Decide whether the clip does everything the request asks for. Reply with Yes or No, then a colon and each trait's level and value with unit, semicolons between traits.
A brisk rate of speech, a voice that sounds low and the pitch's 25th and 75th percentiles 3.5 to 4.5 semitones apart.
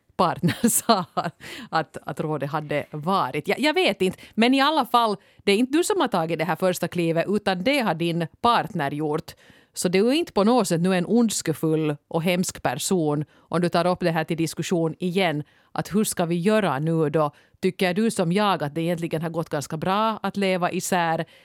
No: fast, 215 wpm; medium, 175 Hz; average, 4.0 semitones